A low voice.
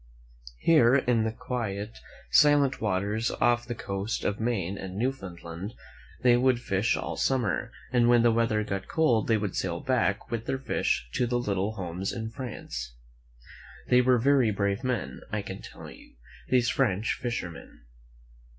Yes: low, 115 Hz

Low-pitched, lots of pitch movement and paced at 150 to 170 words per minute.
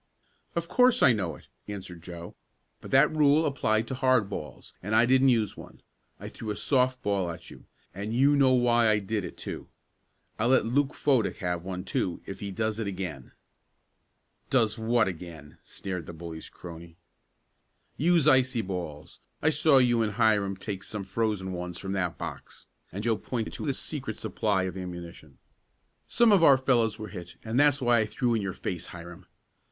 No: low, 110 Hz; wide, 5.8 semitones; average, 185 wpm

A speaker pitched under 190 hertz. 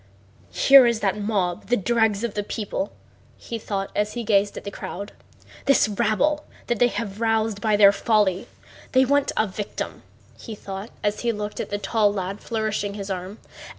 No: high, 210 Hz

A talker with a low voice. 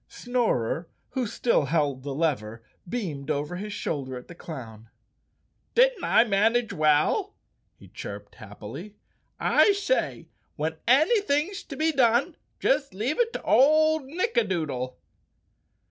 No: high, 200 Hz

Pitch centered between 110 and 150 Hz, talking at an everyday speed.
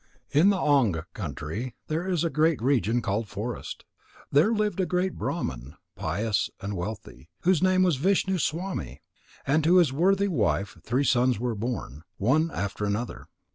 Yes: low, 135 Hz; average, 155 wpm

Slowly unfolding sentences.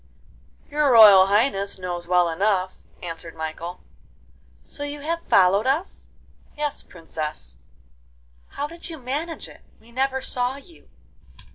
Yes: slow, 125 wpm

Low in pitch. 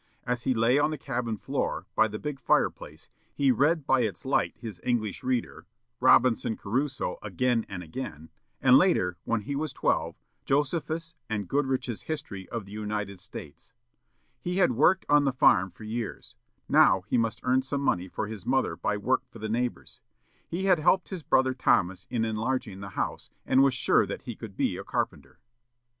Yes: low, 125 Hz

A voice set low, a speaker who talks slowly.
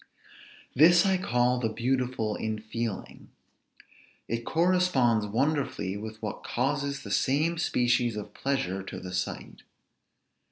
Yes: low, 120 Hz; slow, 120 wpm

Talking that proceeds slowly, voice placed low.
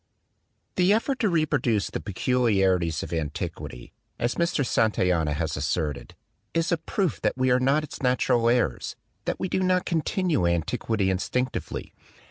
No: average, 145 wpm; low, 120 Hz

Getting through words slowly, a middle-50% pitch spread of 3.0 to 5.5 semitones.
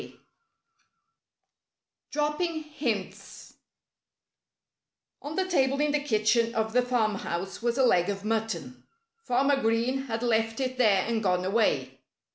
Yes: slow, 125 wpm; average, 4.1 semitones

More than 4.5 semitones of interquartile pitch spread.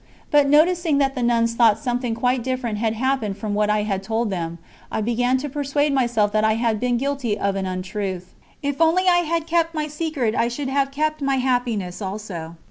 Yes: average, 5.0 semitones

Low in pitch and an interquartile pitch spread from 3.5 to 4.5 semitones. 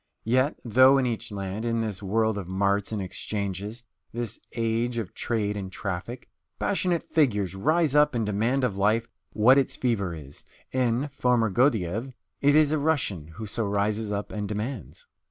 Yes: low, 110 Hz; average, 4.1 semitones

